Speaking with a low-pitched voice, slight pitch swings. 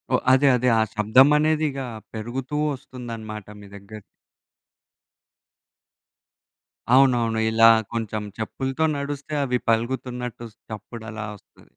No: low, 120 Hz; average, 3.2 semitones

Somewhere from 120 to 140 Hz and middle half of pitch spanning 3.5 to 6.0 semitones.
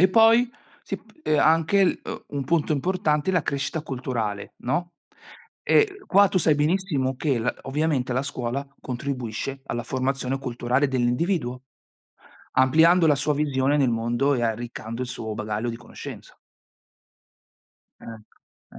Yes: low, 135 Hz; average, 4.6 semitones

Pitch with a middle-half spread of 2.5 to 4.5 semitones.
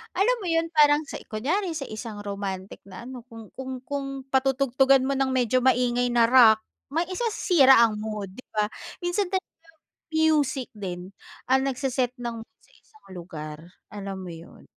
No: average, 5.2 semitones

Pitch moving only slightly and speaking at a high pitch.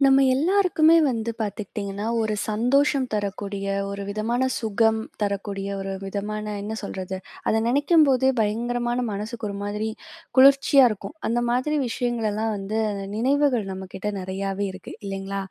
No: average, 3.8 semitones; high, 220 Hz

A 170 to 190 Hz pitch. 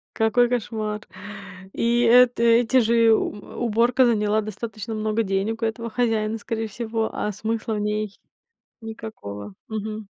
No: high, 220 Hz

